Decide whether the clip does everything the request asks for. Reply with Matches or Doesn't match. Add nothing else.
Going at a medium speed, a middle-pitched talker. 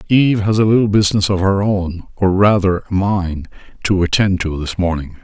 Doesn't match